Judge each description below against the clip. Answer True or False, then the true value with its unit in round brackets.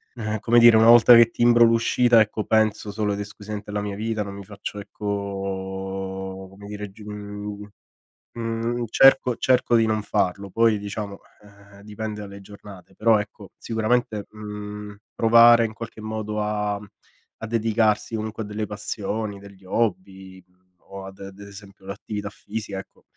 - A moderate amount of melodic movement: False (1.9 semitones)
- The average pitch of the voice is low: True (105 Hz)